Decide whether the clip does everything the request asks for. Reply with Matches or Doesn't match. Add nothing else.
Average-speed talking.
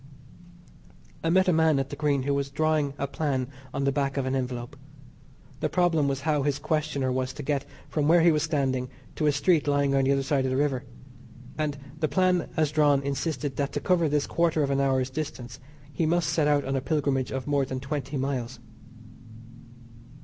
Doesn't match